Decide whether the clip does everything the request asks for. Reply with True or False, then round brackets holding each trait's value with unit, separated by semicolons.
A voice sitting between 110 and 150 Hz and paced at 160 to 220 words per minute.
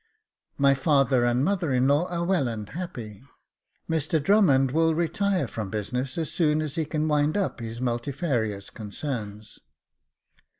False (140 Hz; 145 wpm)